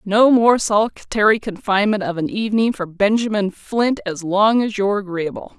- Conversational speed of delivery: Yes, average, 170 wpm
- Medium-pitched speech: No, high, 205 Hz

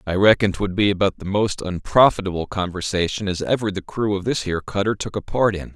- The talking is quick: Yes, fast, 220 wpm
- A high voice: No, low, 100 Hz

